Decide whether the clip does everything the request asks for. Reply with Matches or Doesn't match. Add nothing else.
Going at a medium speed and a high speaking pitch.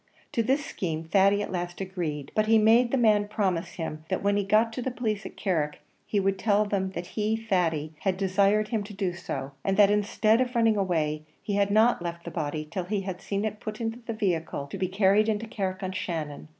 Doesn't match